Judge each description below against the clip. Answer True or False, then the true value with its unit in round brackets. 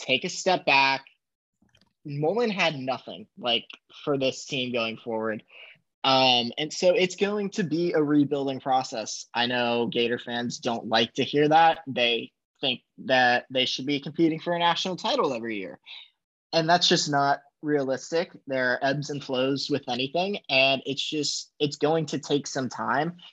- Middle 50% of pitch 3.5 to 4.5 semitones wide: True (4.1 semitones)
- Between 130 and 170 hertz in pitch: True (140 Hz)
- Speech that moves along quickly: False (170 wpm)